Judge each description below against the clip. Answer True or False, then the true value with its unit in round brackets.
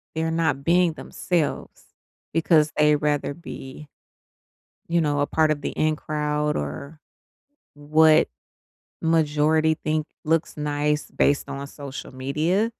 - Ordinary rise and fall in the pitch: False (1.7 semitones)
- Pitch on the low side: False (150 Hz)